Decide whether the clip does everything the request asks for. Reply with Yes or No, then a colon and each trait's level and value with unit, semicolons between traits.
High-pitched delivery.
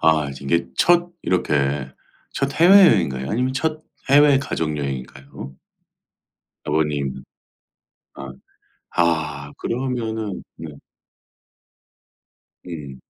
No: very low, 80 Hz